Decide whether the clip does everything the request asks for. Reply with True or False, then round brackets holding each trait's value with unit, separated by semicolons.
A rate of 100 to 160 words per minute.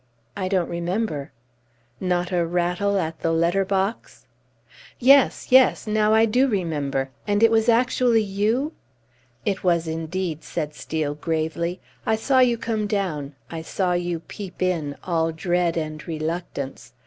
True (145 wpm)